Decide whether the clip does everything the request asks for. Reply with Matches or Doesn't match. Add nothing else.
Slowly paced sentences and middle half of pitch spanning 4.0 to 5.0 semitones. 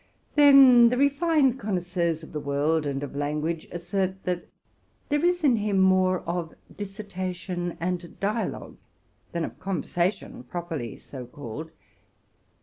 Matches